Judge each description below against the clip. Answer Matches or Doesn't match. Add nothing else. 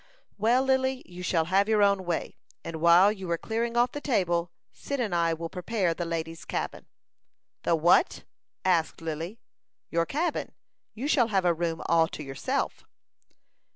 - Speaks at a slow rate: Doesn't match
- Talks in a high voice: Doesn't match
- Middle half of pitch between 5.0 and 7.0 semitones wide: Matches